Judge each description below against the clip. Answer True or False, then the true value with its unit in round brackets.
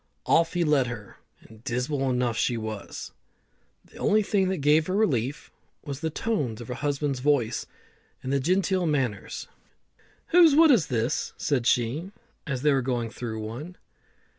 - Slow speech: False (165 wpm)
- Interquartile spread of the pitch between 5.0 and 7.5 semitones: True (5.5 semitones)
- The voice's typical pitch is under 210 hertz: True (140 Hz)